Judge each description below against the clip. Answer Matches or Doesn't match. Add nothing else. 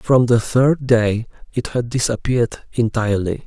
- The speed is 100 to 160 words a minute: Matches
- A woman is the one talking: Doesn't match